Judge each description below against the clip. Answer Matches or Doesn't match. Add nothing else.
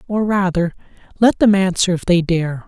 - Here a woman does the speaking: Doesn't match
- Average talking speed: Matches